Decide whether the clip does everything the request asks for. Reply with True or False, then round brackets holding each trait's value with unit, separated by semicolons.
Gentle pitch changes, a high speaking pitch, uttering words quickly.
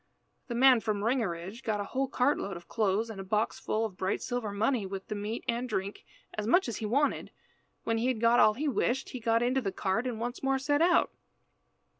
False (3.5 semitones; 230 Hz; 225 wpm)